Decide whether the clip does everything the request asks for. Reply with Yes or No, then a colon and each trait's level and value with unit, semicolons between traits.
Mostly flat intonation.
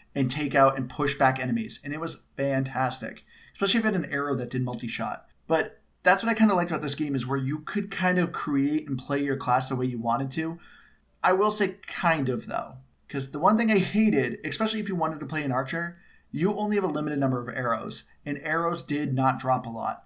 No: average, 4.8 semitones